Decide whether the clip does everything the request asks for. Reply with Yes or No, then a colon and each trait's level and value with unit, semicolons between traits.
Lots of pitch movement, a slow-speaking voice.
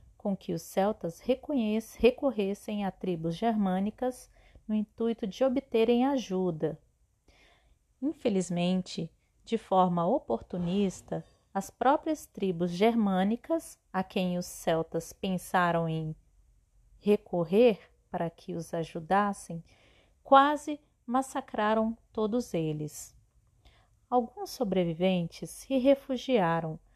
Yes: wide, 5.8 semitones; slow, 90 wpm